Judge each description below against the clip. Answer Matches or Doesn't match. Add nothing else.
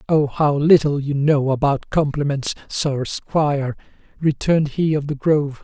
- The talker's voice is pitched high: Doesn't match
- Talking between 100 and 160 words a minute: Matches